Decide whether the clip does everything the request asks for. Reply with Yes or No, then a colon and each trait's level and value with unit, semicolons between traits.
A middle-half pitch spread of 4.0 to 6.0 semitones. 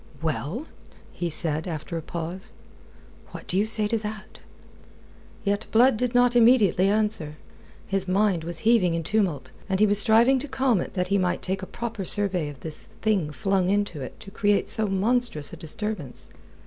Yes: average, 4.3 semitones